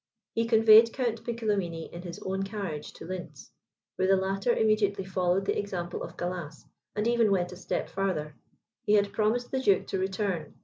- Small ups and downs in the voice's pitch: No, average, 3.3 semitones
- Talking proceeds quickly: No, average, 180 wpm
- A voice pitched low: No, high, 195 Hz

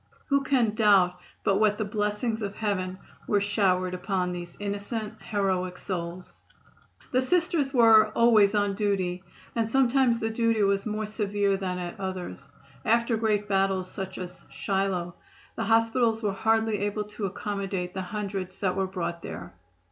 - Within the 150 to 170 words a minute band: Yes, average, 155 wpm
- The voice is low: No, high, 205 Hz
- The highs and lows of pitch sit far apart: No, average, 2.9 semitones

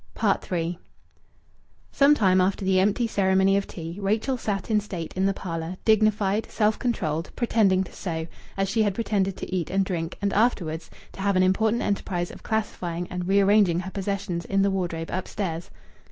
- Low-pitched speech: No, high, 195 Hz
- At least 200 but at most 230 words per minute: No, average, 175 wpm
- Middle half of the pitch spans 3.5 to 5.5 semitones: No, average, 2.7 semitones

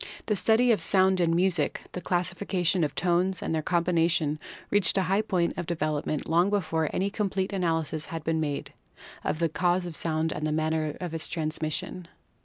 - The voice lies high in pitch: No, medium, 170 Hz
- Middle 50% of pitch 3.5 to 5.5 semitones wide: No, average, 2.9 semitones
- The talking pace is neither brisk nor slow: Yes, average, 185 wpm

